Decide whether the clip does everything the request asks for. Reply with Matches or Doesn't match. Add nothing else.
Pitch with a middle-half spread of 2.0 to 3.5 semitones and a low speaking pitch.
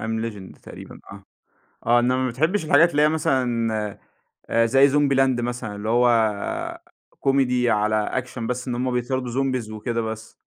Matches